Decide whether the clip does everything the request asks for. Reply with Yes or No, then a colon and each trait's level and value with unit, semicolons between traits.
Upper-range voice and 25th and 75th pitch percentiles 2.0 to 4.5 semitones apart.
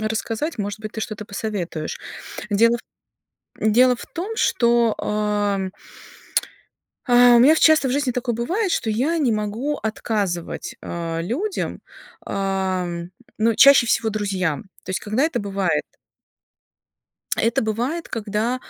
Yes: high, 220 Hz; average, 3.7 semitones